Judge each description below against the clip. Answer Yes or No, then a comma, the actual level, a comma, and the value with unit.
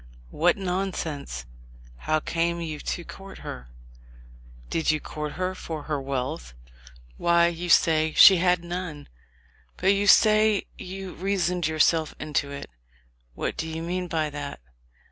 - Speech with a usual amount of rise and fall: Yes, average, 3.2 semitones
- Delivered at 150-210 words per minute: No, average, 140 wpm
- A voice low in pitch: No, medium, 165 Hz